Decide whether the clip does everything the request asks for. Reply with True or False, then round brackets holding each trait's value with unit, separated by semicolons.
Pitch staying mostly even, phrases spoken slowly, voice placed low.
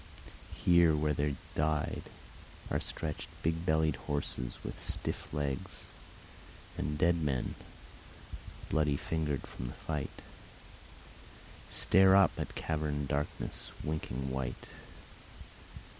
True (2.0 semitones; 100 wpm; 75 Hz)